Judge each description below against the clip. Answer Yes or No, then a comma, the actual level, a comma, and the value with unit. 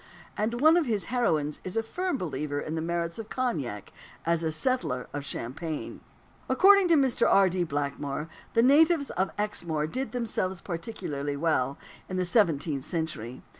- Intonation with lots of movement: Yes, wide, 7.9 semitones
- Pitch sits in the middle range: Yes, medium, 170 Hz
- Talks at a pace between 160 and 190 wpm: Yes, average, 165 wpm